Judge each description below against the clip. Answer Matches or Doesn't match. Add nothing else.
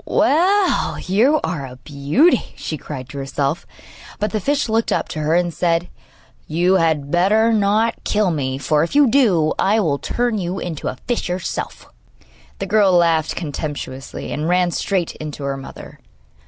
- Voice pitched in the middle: Matches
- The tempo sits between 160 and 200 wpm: Matches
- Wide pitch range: Matches